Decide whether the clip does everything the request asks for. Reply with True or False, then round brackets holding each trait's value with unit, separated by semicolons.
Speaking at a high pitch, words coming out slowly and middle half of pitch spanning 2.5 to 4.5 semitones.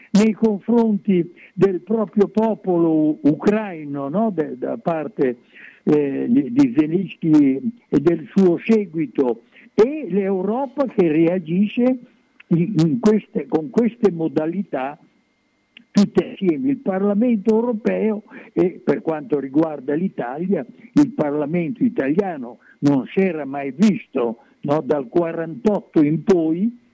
False (200 Hz; 110 wpm; 5.6 semitones)